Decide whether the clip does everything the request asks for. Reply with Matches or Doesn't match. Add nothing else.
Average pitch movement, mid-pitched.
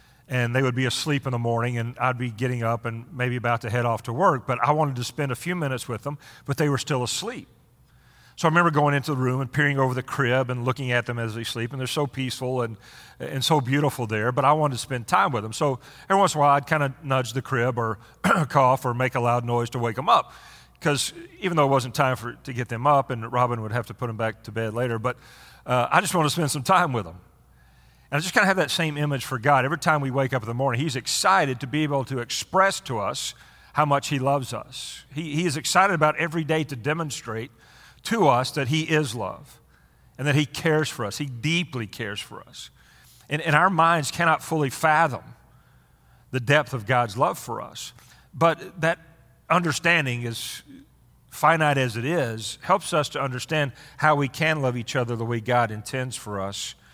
Doesn't match